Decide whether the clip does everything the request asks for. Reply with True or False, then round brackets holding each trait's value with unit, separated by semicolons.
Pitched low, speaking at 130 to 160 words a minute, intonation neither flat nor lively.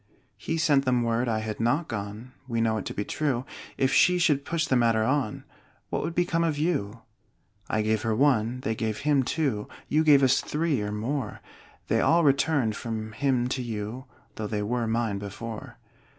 False (120 Hz; 195 wpm; 4.9 semitones)